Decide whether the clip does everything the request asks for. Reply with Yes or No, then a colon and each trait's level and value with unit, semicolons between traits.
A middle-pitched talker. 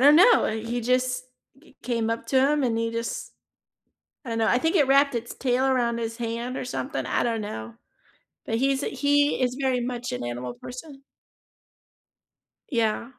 No: high, 245 Hz